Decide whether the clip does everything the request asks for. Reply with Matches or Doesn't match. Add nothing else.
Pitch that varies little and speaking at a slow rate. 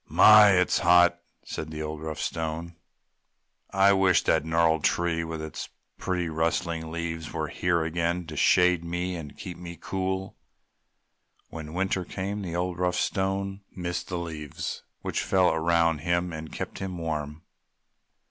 Doesn't match